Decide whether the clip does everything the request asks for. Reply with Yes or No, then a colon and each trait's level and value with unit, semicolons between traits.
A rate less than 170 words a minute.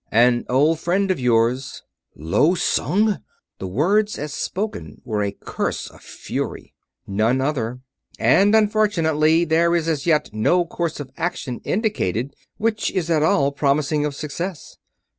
Yes: average, 140 wpm